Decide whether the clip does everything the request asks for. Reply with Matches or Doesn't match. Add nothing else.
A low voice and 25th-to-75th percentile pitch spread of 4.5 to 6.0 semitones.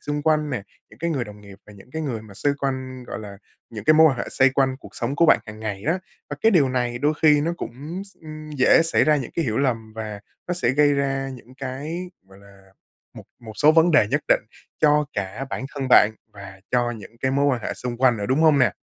Matches